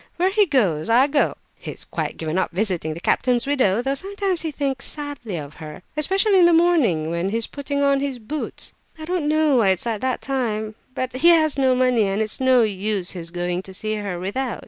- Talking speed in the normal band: No, fast, 215 wpm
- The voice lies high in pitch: Yes, very high, 250 Hz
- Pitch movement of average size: No, wide, 7.0 semitones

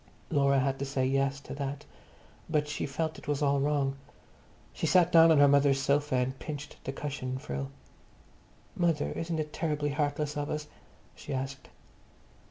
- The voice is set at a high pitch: No, medium, 145 Hz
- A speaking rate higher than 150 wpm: Yes, average, 170 wpm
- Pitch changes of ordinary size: No, narrow, 1.7 semitones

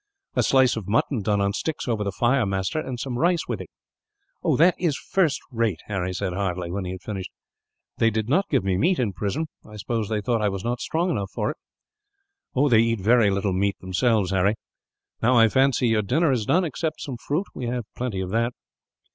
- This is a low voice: Yes, low, 115 Hz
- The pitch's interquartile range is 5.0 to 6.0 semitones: Yes, wide, 5.4 semitones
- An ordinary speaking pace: No, fast, 220 wpm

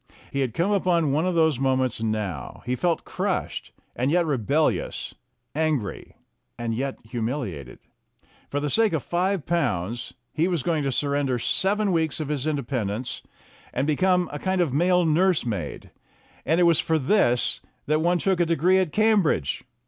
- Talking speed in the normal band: Yes, average, 170 wpm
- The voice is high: No, medium, 150 Hz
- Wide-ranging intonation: Yes, wide, 5.7 semitones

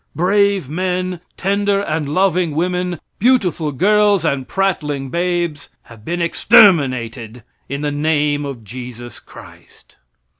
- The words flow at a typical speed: No, slow, 115 wpm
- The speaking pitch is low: No, medium, 165 Hz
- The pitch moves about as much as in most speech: Yes, average, 4.8 semitones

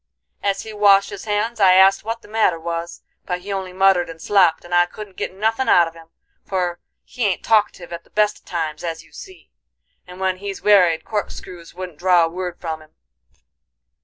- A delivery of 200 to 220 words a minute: Yes, fast, 205 wpm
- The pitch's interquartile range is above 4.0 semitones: No, average, 3.1 semitones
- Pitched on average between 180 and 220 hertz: Yes, medium, 185 Hz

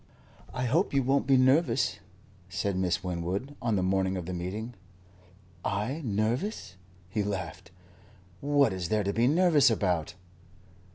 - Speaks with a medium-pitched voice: No, low, 105 Hz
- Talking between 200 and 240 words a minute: No, average, 145 wpm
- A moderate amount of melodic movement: No, wide, 6.4 semitones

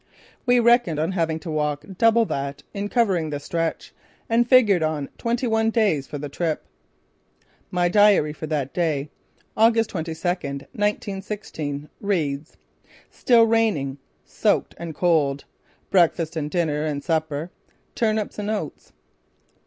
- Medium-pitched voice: Yes, medium, 170 Hz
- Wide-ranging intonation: Yes, wide, 6.1 semitones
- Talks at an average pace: No, slow, 130 wpm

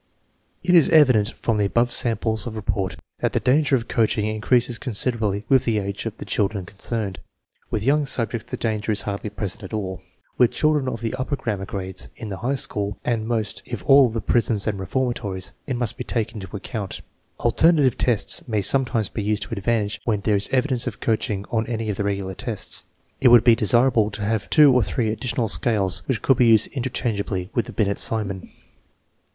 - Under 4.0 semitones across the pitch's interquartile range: Yes, average, 3.2 semitones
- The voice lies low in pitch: Yes, low, 110 Hz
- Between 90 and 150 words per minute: No, average, 200 wpm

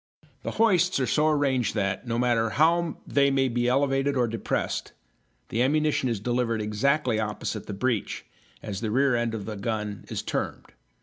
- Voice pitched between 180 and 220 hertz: No, low, 120 Hz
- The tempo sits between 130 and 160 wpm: No, average, 175 wpm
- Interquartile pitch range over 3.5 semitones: Yes, average, 4.2 semitones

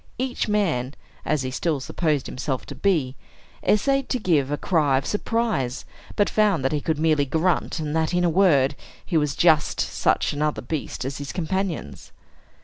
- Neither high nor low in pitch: Yes, medium, 155 Hz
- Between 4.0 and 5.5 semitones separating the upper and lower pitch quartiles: Yes, average, 5.2 semitones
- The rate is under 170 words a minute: No, average, 175 wpm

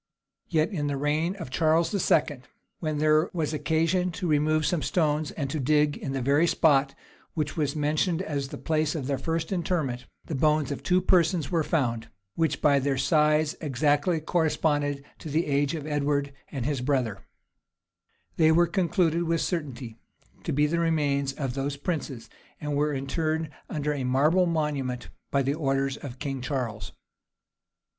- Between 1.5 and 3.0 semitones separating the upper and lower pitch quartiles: Yes, narrow, 2.6 semitones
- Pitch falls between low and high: Yes, medium, 150 Hz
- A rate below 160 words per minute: No, average, 165 wpm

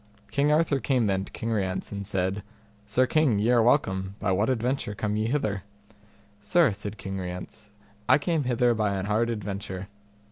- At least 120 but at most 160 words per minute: No, average, 180 wpm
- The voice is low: Yes, low, 105 Hz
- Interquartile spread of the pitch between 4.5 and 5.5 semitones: No, average, 4.1 semitones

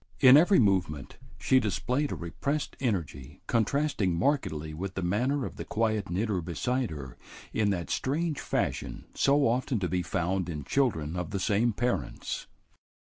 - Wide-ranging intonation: Yes, wide, 7.0 semitones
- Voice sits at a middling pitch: No, low, 105 Hz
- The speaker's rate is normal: Yes, average, 155 wpm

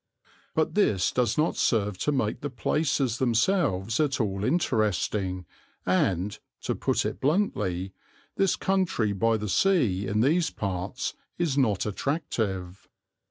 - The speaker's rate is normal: No, slow, 130 wpm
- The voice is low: Yes, low, 110 Hz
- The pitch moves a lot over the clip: Yes, wide, 7.1 semitones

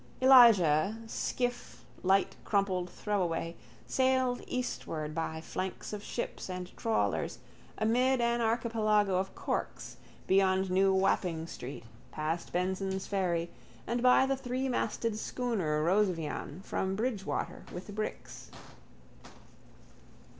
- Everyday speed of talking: No, slow, 105 wpm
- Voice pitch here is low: No, high, 195 Hz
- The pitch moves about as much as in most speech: Yes, average, 4.7 semitones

